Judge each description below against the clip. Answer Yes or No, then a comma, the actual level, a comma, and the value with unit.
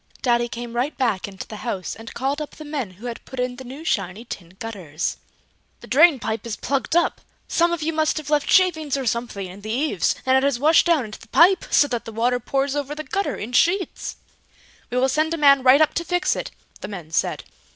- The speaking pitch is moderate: No, very high, 260 Hz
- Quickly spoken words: Yes, fast, 235 wpm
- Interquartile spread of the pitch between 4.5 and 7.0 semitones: Yes, average, 5.2 semitones